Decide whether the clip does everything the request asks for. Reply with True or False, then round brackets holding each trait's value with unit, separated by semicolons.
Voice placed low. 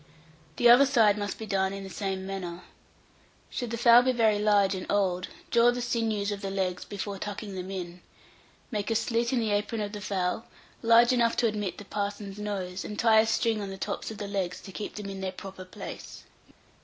False (205 Hz)